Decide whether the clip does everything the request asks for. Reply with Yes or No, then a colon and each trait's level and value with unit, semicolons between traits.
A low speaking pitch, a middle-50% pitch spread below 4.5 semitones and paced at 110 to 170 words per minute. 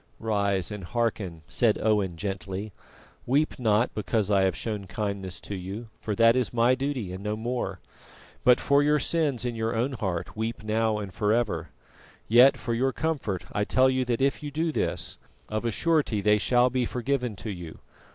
No: low, 110 Hz; average, 3.9 semitones; average, 185 wpm